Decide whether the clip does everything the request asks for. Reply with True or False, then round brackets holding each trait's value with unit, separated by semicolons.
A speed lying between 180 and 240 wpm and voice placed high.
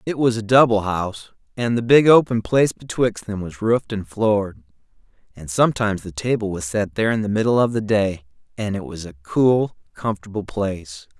False (195 wpm; 105 Hz)